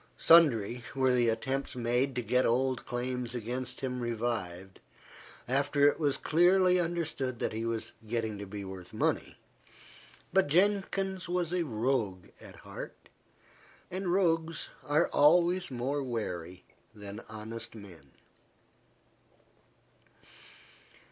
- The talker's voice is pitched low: Yes, low, 125 Hz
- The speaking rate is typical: No, slow, 115 wpm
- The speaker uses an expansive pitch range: Yes, wide, 6.3 semitones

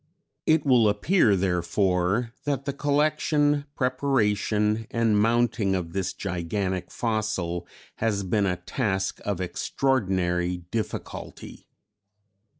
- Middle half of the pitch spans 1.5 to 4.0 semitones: No, wide, 5.4 semitones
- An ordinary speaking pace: No, slow, 105 wpm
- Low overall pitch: Yes, low, 105 Hz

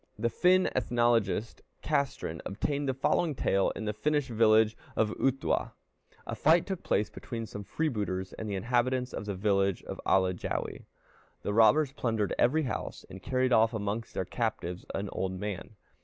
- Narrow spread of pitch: No, average, 4.5 semitones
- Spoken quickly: No, average, 160 wpm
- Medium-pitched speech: No, low, 115 Hz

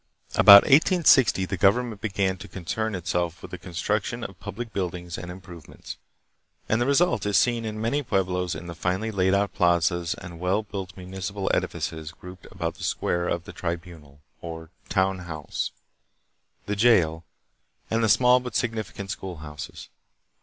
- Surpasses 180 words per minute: No, average, 155 wpm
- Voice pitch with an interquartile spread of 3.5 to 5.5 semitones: Yes, average, 3.8 semitones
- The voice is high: No, very low, 95 Hz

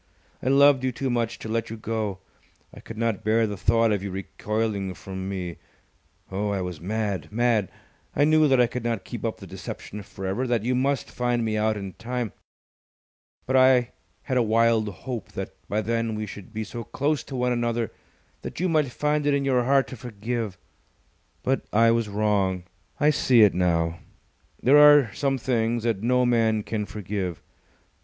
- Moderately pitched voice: No, low, 115 Hz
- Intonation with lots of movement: No, average, 3.4 semitones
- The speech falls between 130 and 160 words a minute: No, average, 190 wpm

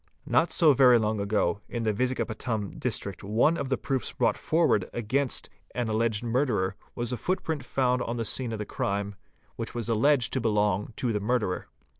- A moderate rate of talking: Yes, average, 185 wpm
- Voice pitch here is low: Yes, low, 115 Hz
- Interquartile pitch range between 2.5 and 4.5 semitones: Yes, average, 3.4 semitones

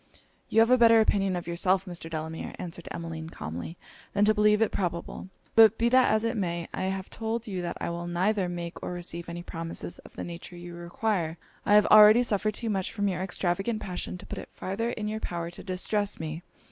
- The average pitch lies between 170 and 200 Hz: Yes, medium, 185 Hz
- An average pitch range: Yes, average, 3.8 semitones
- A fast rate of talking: Yes, fast, 220 wpm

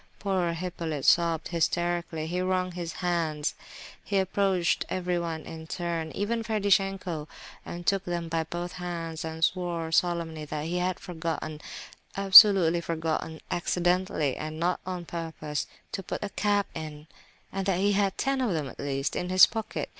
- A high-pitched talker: No, medium, 175 Hz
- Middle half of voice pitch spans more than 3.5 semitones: No, narrow, 2.5 semitones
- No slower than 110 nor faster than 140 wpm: Yes, slow, 135 wpm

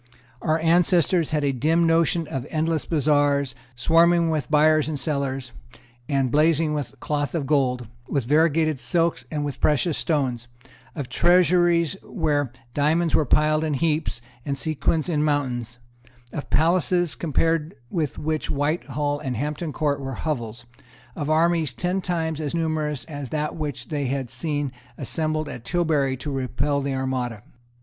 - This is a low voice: No, medium, 150 Hz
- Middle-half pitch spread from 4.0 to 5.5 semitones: No, average, 2.8 semitones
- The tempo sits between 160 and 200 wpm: No, average, 150 wpm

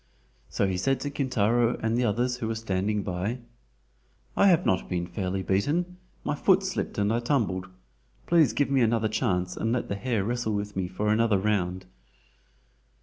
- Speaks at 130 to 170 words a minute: No, average, 180 wpm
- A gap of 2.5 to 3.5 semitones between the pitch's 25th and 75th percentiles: No, average, 4.4 semitones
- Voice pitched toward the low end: Yes, low, 110 Hz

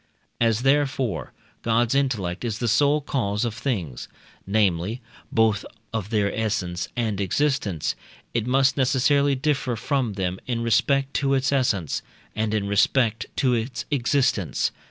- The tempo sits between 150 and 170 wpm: No, slow, 135 wpm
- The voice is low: Yes, low, 115 Hz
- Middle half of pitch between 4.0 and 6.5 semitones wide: Yes, average, 4.6 semitones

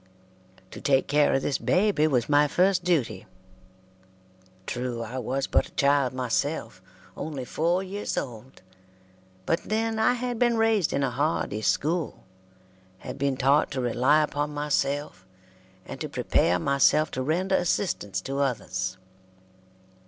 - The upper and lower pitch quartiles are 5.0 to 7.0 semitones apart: Yes, average, 5.3 semitones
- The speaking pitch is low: No, medium, 145 Hz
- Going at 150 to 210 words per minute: No, average, 140 wpm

